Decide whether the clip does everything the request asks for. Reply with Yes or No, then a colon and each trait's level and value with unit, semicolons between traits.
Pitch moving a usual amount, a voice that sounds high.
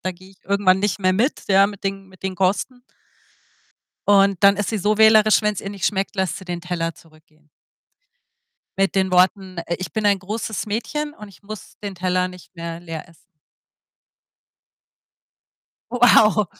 No: narrow, 2.3 semitones; high, 195 Hz